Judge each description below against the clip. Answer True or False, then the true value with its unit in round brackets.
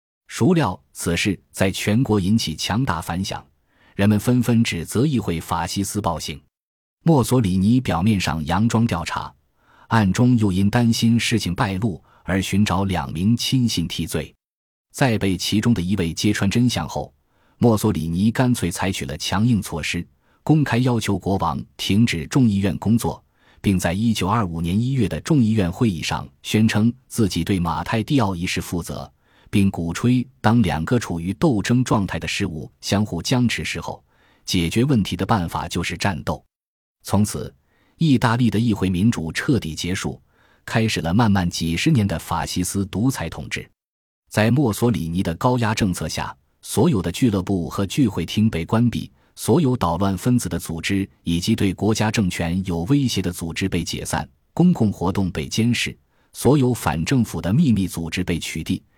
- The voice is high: False (100 Hz)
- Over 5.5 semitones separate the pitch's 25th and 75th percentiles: False (5.2 semitones)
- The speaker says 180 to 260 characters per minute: True (255 characters per minute)